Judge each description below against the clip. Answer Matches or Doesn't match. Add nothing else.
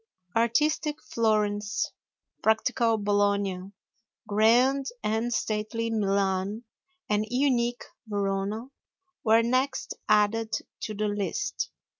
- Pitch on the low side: Doesn't match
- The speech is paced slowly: Matches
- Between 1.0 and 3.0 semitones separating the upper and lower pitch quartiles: Matches